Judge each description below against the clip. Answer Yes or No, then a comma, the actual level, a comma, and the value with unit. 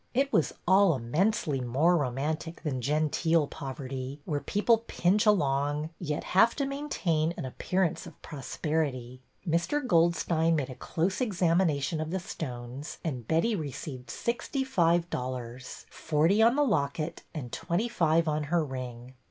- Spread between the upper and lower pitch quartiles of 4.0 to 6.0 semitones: Yes, average, 4.9 semitones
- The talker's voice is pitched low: No, medium, 160 Hz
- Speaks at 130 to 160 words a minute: Yes, average, 145 wpm